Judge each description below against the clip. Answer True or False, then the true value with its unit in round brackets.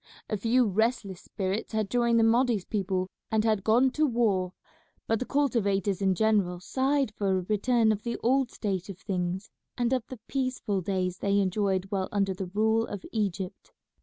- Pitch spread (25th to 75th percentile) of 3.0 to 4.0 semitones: True (3.6 semitones)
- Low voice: False (210 Hz)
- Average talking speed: True (185 wpm)